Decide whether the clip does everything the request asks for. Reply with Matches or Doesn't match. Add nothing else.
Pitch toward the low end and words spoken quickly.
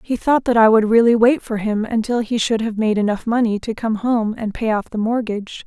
Doesn't match